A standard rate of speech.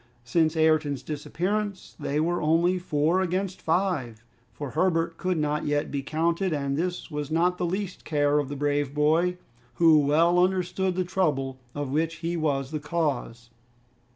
Yes: average, 160 wpm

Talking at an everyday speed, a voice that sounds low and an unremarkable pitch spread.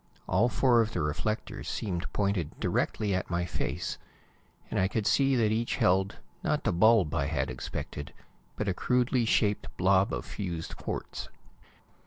Yes: average, 160 wpm; low, 100 Hz; average, 4.3 semitones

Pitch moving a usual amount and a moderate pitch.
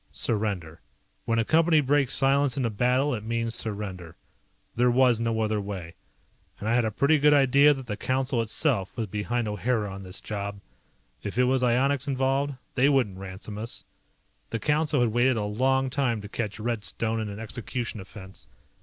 No: average, 4.2 semitones; low, 115 Hz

